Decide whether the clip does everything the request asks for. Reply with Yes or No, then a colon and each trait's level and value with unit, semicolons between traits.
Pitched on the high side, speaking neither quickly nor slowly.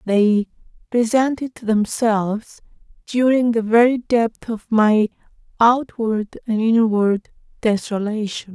No: high, 225 Hz; slow, 90 wpm